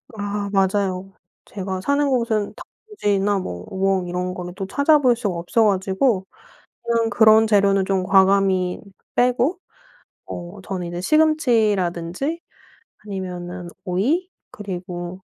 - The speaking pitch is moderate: No, high, 195 Hz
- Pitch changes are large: No, average, 3.6 semitones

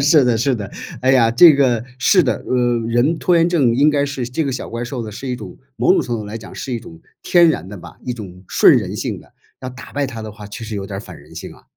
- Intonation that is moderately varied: Yes, average, 3.7 semitones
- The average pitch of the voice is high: No, low, 125 Hz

